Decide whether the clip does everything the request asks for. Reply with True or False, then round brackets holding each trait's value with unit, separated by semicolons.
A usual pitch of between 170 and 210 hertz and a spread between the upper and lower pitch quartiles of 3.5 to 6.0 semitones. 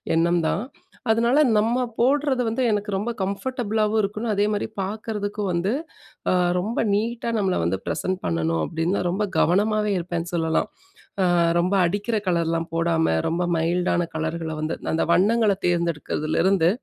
True (190 Hz; 4.3 semitones)